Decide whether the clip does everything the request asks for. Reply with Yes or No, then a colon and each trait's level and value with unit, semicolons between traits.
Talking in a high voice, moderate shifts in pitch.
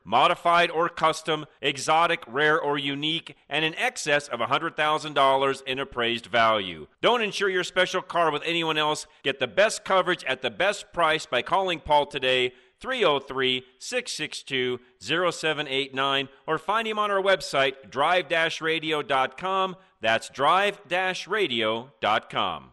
No: medium, 155 Hz; average, 4.6 semitones